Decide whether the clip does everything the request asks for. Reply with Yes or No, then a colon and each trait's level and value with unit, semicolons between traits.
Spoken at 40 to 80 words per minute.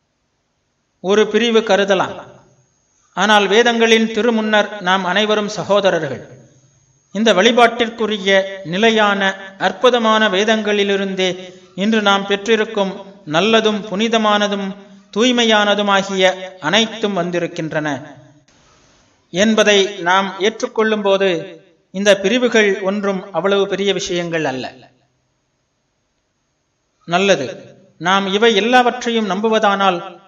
Yes: slow, 75 wpm